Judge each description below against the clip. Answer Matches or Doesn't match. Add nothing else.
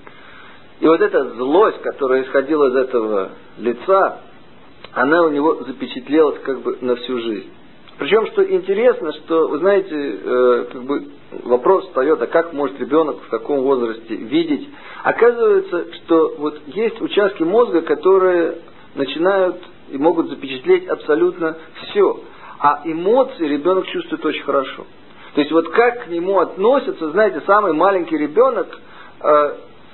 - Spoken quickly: Doesn't match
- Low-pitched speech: Doesn't match